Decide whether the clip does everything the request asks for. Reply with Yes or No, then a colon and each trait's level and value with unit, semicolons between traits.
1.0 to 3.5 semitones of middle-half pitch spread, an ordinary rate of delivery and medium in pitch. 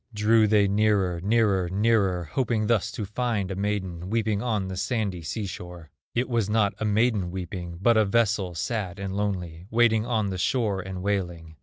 No: average, 3.0 semitones; average, 180 wpm; low, 100 Hz